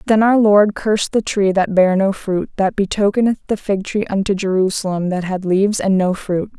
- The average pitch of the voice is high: Yes, high, 200 Hz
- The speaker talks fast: Yes, fast, 210 wpm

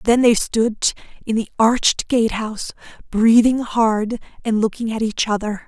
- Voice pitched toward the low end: No, high, 225 Hz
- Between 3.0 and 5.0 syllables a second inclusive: Yes, 4.5 syllables/s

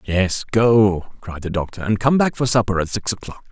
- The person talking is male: Yes, male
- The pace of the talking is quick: Yes, fast, 220 wpm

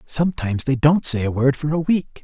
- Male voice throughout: Yes, male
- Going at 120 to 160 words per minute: No, fast, 240 wpm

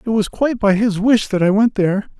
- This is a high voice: Yes, high, 210 Hz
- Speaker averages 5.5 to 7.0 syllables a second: Yes, 6.1 syllables/s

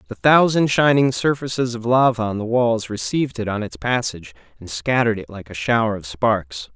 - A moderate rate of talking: Yes, average, 195 wpm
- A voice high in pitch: No, low, 115 Hz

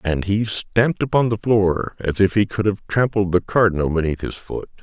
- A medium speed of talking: No, fast, 210 wpm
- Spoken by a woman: No, male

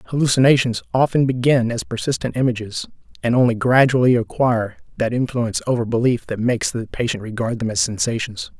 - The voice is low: Yes, low, 120 Hz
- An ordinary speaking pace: Yes, average, 155 wpm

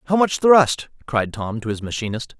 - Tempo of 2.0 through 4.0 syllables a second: No, 4.9 syllables/s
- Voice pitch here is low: Yes, low, 130 Hz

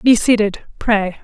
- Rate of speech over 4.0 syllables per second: No, 3.9 syllables/s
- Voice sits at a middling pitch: No, high, 215 Hz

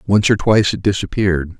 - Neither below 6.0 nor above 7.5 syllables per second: Yes, 6.3 syllables/s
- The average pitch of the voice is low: Yes, low, 100 Hz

